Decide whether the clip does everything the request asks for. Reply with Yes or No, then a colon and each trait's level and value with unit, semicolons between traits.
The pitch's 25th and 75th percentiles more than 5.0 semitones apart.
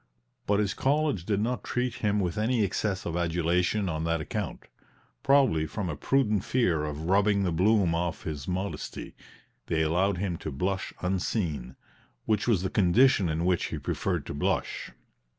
No: average, 4.2 semitones